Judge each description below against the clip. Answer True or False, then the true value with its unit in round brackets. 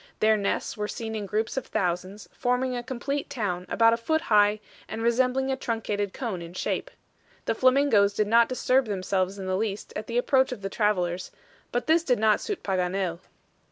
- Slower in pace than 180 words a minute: False (190 wpm)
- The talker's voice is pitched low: False (220 Hz)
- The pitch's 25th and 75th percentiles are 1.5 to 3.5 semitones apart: False (4.1 semitones)